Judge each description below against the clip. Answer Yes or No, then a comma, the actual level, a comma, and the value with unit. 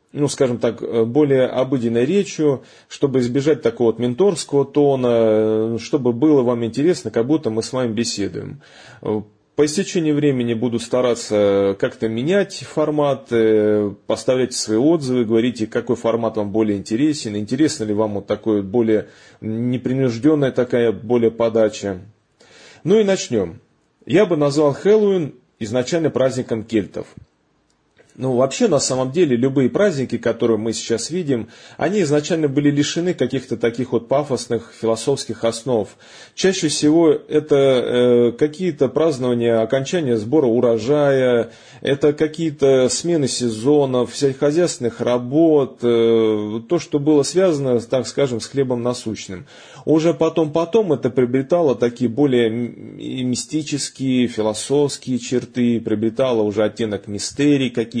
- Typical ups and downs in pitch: Yes, average, 4.2 semitones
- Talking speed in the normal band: Yes, average, 125 wpm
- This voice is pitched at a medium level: No, low, 125 Hz